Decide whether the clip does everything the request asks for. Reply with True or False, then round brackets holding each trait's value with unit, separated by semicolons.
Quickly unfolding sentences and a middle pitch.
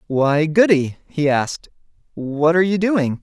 False (150 wpm; 160 Hz)